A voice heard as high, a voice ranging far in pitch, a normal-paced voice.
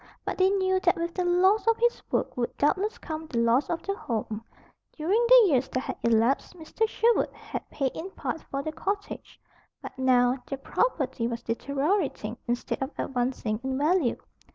Yes: very high, 300 Hz; wide, 7.0 semitones; average, 180 wpm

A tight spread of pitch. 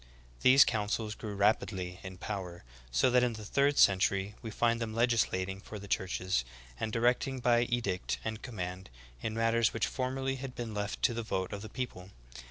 No: average, 3.8 semitones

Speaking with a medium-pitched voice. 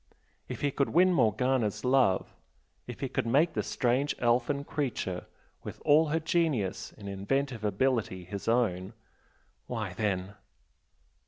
No: low, 120 Hz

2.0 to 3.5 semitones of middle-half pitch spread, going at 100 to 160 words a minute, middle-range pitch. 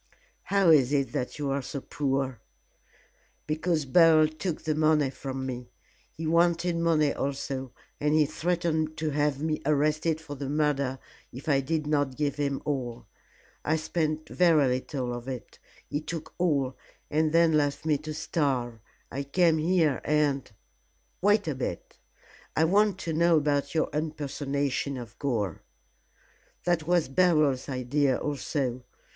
Yes: average, 2.7 semitones; average, 150 wpm; medium, 150 Hz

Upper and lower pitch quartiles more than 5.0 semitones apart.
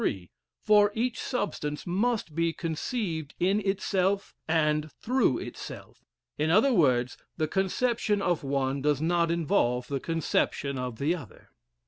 Yes: wide, 5.6 semitones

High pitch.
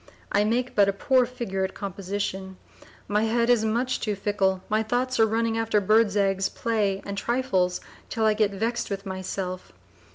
Yes: high, 210 Hz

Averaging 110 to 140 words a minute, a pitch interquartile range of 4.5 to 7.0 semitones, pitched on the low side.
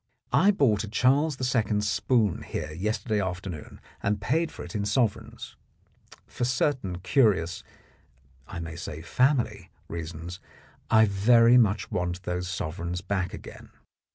Yes: slow, 135 wpm; average, 5.1 semitones; low, 100 Hz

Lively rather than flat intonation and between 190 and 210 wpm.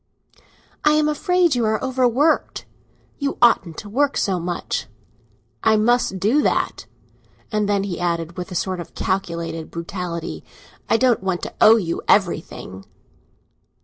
No: wide, 6.1 semitones; average, 145 wpm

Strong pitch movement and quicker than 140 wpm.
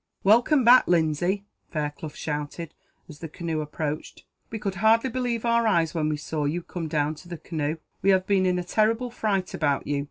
Yes: wide, 5.7 semitones; average, 195 wpm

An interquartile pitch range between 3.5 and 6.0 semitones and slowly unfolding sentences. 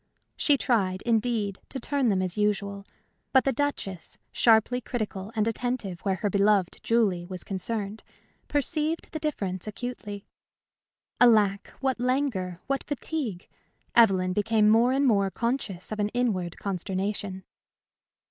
Yes: average, 4.3 semitones; slow, 130 wpm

